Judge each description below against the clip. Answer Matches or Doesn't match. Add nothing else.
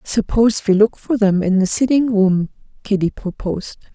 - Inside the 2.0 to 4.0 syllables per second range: Doesn't match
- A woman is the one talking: Matches